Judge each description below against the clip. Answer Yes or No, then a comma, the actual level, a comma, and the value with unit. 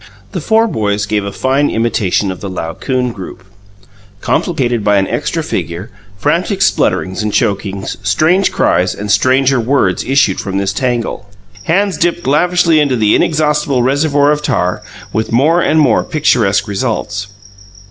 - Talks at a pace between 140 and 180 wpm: Yes, average, 145 wpm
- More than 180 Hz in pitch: No, low, 120 Hz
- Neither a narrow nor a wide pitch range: No, wide, 6.9 semitones